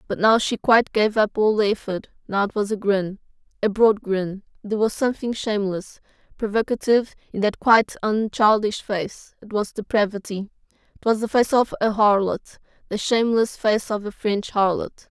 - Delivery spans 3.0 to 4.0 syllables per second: No, 5.3 syllables/s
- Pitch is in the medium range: No, high, 210 Hz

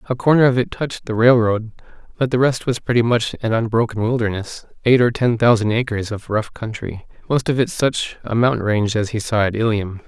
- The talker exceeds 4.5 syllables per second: Yes, 5.6 syllables/s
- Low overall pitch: Yes, low, 115 Hz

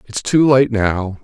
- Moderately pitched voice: No, low, 115 Hz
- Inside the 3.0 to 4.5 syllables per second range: Yes, 3.7 syllables/s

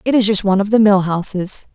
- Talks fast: Yes, fast, 275 wpm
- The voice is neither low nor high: No, high, 200 Hz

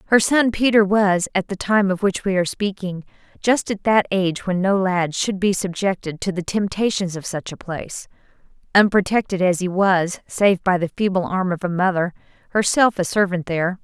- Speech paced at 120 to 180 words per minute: No, average, 195 wpm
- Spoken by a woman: Yes, female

